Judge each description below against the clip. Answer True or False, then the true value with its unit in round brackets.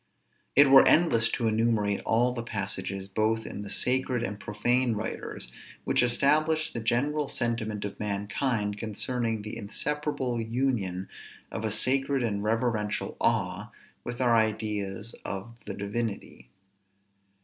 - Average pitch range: True (3.2 semitones)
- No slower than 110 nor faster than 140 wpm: True (135 wpm)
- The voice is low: True (115 Hz)